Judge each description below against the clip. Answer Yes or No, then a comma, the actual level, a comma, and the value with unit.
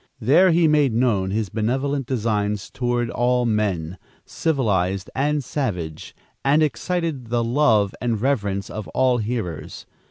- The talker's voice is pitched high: No, low, 120 Hz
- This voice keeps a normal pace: No, slow, 130 wpm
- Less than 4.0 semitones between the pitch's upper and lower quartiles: No, average, 4.8 semitones